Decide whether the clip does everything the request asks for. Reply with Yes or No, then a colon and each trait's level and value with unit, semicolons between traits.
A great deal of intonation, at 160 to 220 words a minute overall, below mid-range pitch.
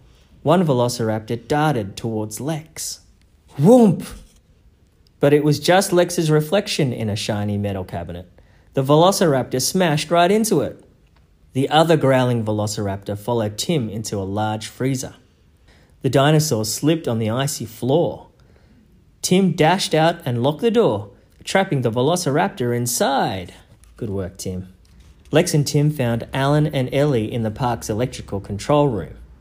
No: wide, 6.8 semitones; slow, 135 wpm; low, 120 Hz